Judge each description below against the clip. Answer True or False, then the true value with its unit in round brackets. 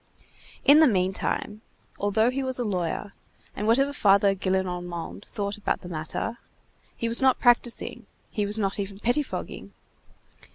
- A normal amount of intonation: True (3.9 semitones)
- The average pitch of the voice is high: True (205 Hz)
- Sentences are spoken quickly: False (140 wpm)